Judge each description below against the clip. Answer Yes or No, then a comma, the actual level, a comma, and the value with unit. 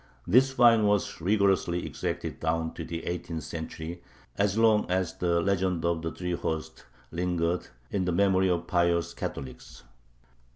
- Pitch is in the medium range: No, very low, 90 Hz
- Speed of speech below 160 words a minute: Yes, average, 150 wpm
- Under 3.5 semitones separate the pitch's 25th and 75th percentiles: Yes, average, 2.7 semitones